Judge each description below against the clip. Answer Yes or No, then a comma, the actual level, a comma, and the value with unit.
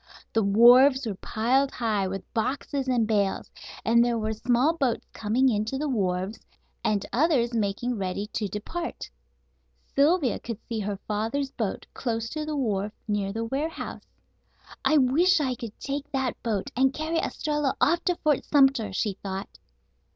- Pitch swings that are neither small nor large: Yes, average, 4.8 semitones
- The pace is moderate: Yes, average, 160 wpm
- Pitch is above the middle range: Yes, high, 235 Hz